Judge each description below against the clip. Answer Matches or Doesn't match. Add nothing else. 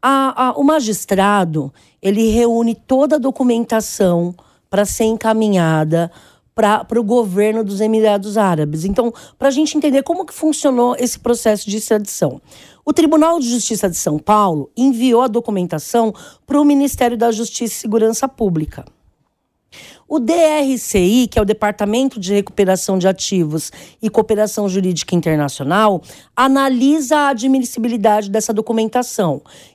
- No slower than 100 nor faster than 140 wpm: Matches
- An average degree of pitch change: Matches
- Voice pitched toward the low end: Doesn't match